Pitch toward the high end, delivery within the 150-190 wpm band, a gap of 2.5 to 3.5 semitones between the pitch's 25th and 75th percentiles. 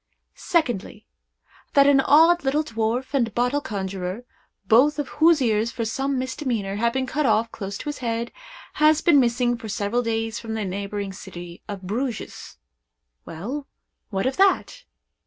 No: high, 235 Hz; average, 155 wpm; average, 4.9 semitones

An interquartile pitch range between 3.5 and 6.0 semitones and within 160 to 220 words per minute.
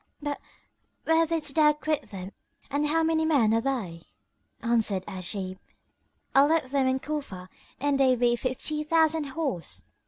No: average, 5.1 semitones; average, 150 wpm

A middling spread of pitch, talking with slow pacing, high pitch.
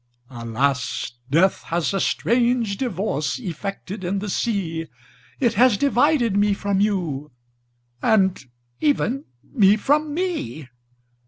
No: wide, 6.2 semitones; slow, 110 wpm; high, 200 Hz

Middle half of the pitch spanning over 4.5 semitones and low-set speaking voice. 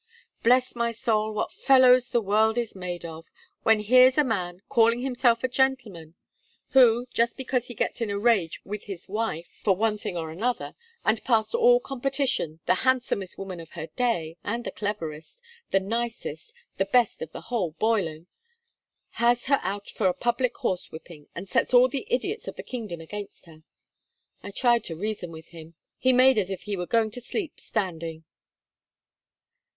No: wide, 5.5 semitones; high, 220 Hz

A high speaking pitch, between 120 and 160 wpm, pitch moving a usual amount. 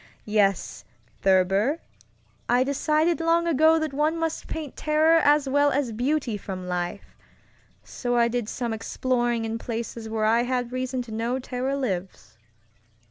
Yes: high, 245 Hz; average, 145 wpm; average, 4.8 semitones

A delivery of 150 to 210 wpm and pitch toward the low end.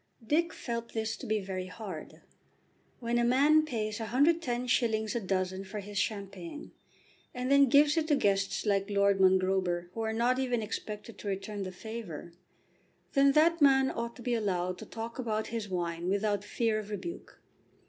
No: average, 170 wpm; high, 220 Hz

